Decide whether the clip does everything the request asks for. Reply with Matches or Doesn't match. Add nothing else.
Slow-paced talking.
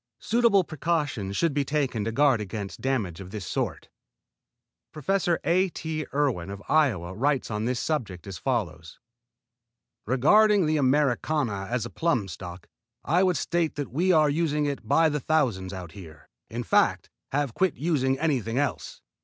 Doesn't match